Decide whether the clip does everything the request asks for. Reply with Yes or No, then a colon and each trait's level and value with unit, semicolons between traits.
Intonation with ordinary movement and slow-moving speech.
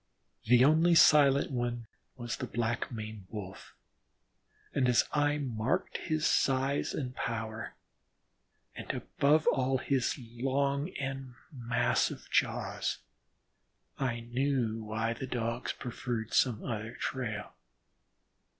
Yes: average, 3.0 semitones; slow, 110 wpm